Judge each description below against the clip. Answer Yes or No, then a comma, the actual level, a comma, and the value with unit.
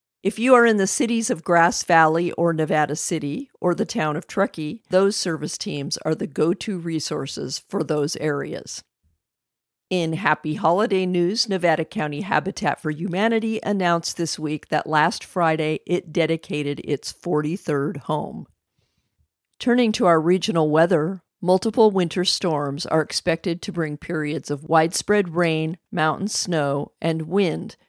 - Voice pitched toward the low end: No, medium, 170 Hz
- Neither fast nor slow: Yes, average, 145 wpm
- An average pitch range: Yes, average, 3.7 semitones